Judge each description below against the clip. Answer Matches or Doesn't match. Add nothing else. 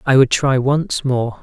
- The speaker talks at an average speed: Doesn't match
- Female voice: Doesn't match